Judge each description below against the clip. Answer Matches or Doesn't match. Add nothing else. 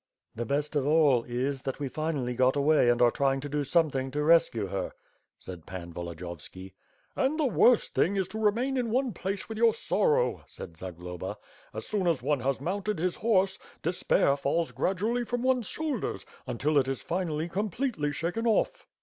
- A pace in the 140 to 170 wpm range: Doesn't match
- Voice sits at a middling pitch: Matches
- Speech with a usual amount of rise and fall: Doesn't match